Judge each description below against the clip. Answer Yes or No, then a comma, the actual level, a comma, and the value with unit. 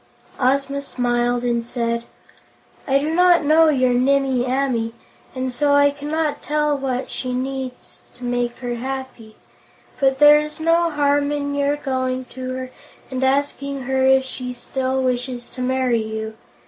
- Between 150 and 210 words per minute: Yes, average, 160 wpm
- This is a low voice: No, very high, 265 Hz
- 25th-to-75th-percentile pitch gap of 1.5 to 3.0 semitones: Yes, narrow, 2.4 semitones